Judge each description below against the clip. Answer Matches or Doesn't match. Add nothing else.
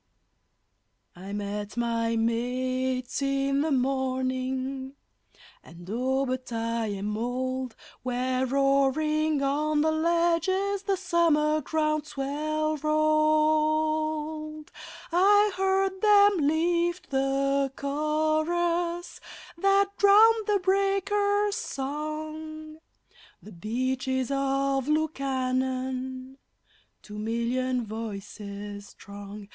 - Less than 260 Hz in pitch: Doesn't match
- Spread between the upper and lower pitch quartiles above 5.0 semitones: Doesn't match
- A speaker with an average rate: Doesn't match